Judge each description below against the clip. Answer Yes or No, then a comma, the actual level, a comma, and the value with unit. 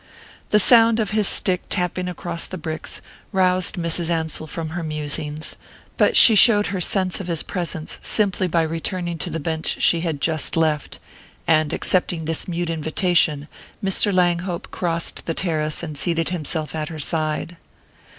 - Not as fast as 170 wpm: Yes, average, 160 wpm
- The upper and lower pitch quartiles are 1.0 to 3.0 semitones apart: Yes, narrow, 2.4 semitones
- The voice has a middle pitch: Yes, medium, 170 Hz